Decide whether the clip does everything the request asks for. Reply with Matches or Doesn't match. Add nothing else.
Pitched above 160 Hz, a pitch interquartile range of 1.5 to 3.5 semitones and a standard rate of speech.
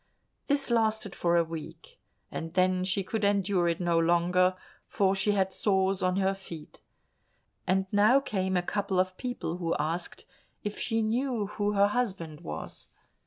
Matches